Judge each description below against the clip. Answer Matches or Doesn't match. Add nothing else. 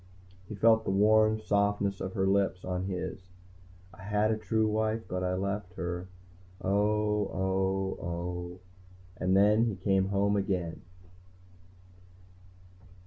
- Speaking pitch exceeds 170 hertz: Doesn't match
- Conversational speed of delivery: Doesn't match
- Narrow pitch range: Matches